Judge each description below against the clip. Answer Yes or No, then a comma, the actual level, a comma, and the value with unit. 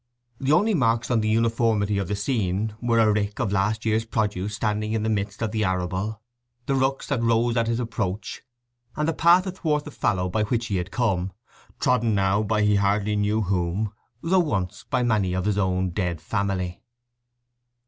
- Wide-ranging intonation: No, average, 2.9 semitones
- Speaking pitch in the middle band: No, low, 110 Hz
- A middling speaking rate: Yes, average, 190 wpm